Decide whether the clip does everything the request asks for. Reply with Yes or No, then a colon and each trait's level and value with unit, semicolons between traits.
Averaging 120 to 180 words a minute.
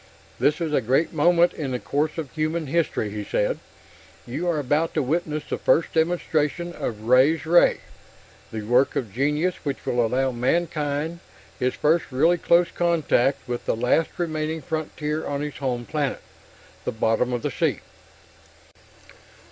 Yes: average, 155 wpm